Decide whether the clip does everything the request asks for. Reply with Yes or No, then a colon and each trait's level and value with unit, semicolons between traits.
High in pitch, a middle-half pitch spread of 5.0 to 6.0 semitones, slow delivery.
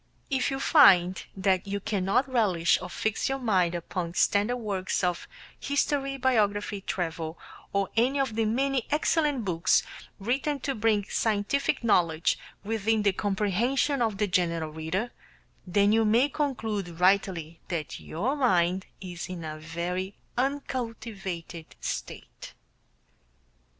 Yes: high, 205 Hz; wide, 5.5 semitones; slow, 130 wpm